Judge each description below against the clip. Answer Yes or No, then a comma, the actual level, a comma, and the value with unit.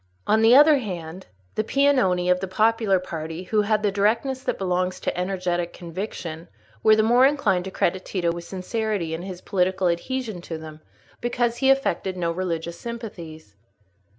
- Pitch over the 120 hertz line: Yes, high, 190 Hz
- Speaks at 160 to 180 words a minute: Yes, average, 170 wpm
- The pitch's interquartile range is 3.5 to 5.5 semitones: Yes, average, 4.4 semitones